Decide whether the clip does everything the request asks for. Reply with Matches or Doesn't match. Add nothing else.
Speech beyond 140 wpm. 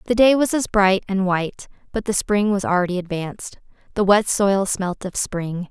Matches